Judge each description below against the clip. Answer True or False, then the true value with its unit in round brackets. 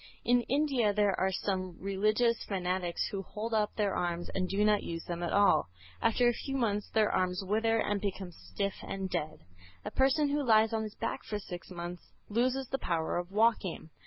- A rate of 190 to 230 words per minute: True (195 wpm)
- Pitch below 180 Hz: False (205 Hz)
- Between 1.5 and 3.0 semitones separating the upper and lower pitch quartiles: False (3.7 semitones)